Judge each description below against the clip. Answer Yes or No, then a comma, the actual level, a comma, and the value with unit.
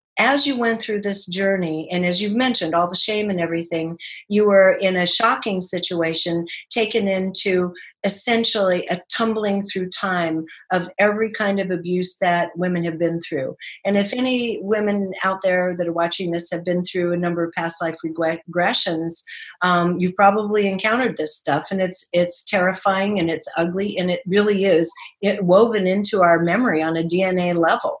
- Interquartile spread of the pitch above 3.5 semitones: No, average, 2.8 semitones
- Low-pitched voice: No, medium, 185 Hz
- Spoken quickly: No, average, 180 wpm